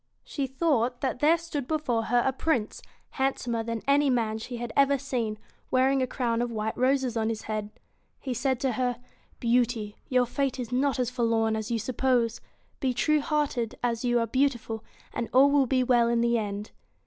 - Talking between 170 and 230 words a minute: Yes, fast, 205 wpm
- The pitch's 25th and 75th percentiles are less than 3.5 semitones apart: Yes, average, 2.7 semitones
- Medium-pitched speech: No, high, 245 Hz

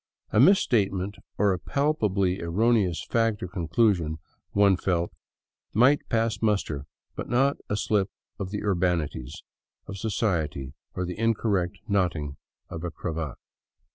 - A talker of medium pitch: No, very low, 95 Hz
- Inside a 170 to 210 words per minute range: No, average, 145 wpm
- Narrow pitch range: No, average, 4.3 semitones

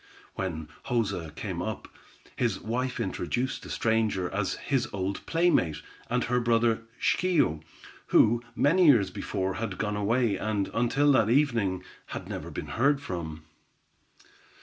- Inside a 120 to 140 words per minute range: Yes, slow, 135 wpm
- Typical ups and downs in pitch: Yes, average, 4.6 semitones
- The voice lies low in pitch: Yes, low, 110 Hz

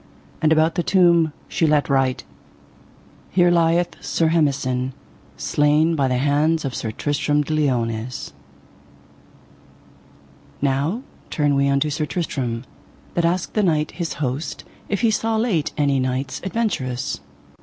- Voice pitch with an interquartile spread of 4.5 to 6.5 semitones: No, average, 3.9 semitones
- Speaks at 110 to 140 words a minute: Yes, slow, 135 wpm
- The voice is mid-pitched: Yes, medium, 150 Hz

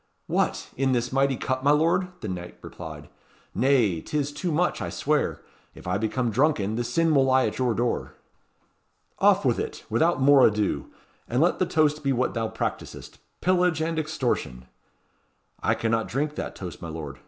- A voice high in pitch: No, low, 130 Hz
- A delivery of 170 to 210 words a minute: Yes, average, 175 wpm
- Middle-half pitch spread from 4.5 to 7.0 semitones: Yes, wide, 5.6 semitones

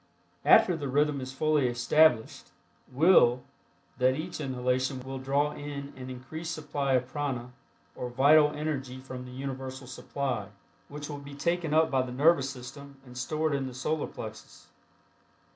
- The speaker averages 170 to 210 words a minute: No, average, 155 wpm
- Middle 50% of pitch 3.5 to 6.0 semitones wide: No, narrow, 2.5 semitones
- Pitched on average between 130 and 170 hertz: Yes, low, 135 Hz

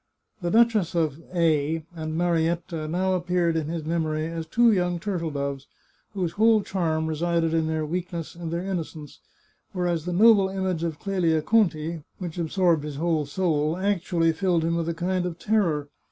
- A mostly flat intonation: Yes, narrow, 2.3 semitones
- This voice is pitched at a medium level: Yes, medium, 170 Hz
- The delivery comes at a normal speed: Yes, average, 170 wpm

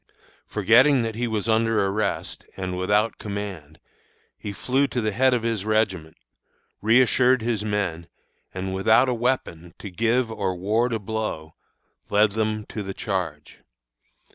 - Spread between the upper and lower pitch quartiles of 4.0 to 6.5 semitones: No, average, 3.2 semitones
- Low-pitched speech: Yes, low, 110 Hz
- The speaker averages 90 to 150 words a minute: Yes, average, 145 wpm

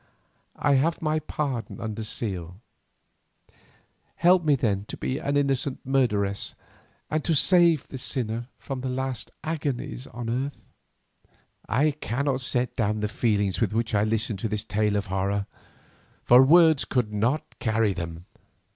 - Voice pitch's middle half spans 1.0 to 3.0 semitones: No, average, 4.9 semitones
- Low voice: Yes, low, 120 Hz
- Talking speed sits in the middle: Yes, average, 145 wpm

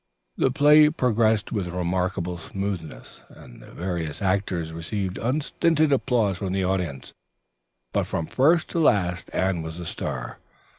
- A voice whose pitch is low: Yes, very low, 95 Hz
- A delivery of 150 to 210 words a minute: No, average, 140 wpm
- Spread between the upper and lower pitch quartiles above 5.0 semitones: Yes, wide, 5.6 semitones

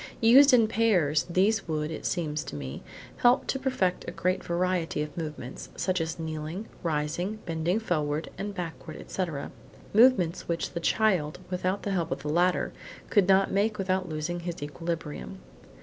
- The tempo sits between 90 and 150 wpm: No, average, 165 wpm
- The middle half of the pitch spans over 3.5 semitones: Yes, average, 3.9 semitones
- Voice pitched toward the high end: No, medium, 175 Hz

